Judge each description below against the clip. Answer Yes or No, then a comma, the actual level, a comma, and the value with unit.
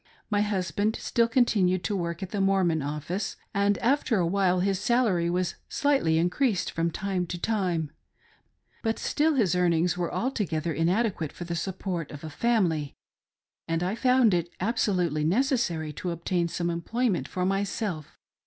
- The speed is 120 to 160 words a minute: Yes, average, 155 wpm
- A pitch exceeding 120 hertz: Yes, medium, 185 Hz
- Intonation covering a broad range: No, average, 4.0 semitones